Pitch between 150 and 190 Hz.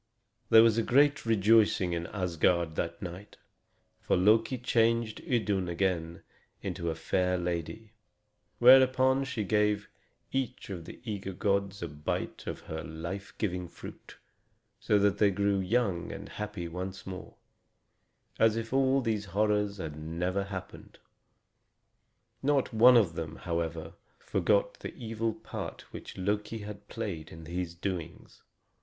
No: low, 100 Hz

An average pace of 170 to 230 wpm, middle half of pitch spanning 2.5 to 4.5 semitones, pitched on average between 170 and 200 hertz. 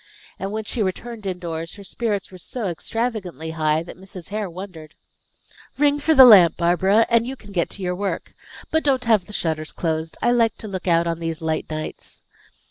No: average, 200 wpm; average, 5.2 semitones; high, 190 Hz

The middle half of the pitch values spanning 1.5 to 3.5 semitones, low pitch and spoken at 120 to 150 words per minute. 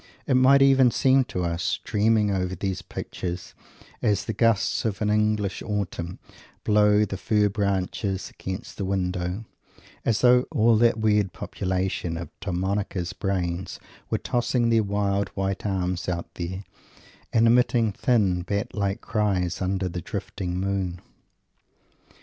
Yes: average, 3.0 semitones; low, 100 Hz; average, 140 wpm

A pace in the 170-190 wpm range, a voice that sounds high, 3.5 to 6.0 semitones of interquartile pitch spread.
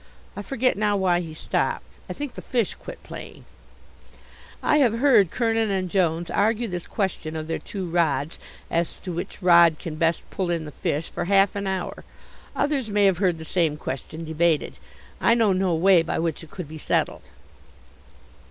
No: average, 185 wpm; medium, 180 Hz; average, 3.9 semitones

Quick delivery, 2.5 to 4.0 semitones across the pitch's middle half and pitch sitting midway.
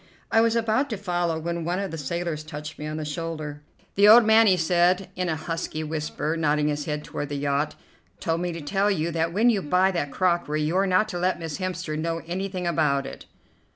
Yes: fast, 220 wpm; average, 3.3 semitones; medium, 170 Hz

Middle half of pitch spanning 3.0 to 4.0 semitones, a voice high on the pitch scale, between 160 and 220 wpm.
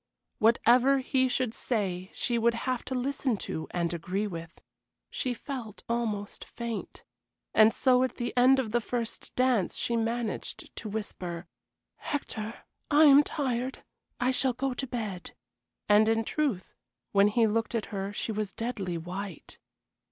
No: average, 3.7 semitones; high, 230 Hz; average, 150 wpm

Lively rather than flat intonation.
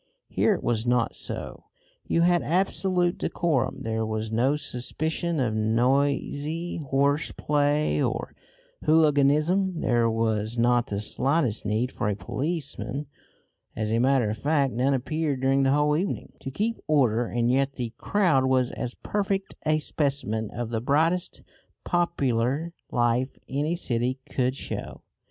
No: average, 4.6 semitones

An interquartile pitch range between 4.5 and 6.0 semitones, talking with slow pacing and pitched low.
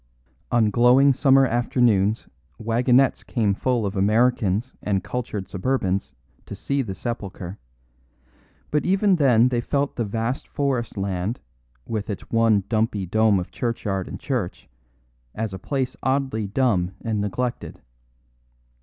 No: average, 4.1 semitones; slow, 130 wpm; low, 115 Hz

